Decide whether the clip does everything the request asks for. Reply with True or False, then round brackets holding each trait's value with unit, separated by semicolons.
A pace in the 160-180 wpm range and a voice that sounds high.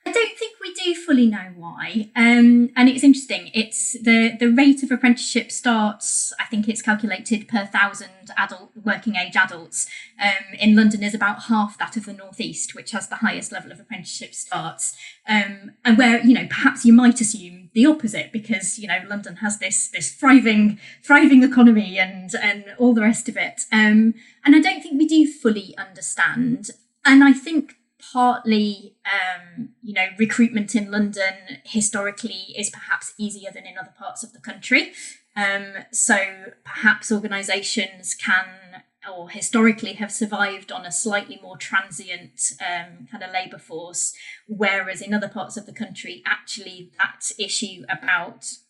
True (165 wpm; 215 Hz)